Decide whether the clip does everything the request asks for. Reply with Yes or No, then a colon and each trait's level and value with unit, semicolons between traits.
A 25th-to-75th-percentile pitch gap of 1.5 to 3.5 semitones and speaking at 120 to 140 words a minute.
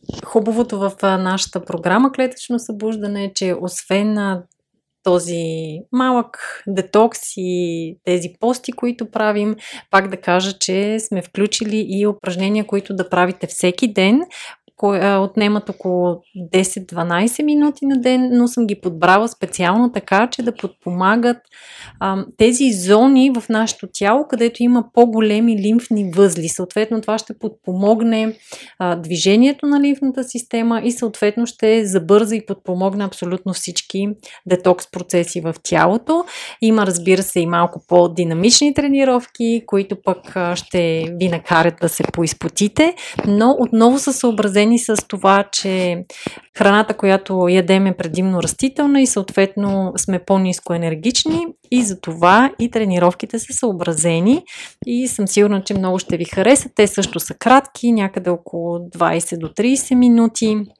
No: average, 4.2 semitones; average, 135 wpm